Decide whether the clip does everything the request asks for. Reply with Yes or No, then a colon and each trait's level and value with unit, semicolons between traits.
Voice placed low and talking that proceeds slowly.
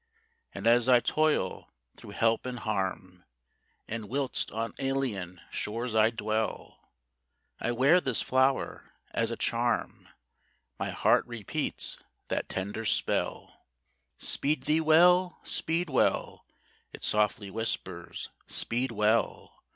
Yes: low, 115 Hz; slow, 115 wpm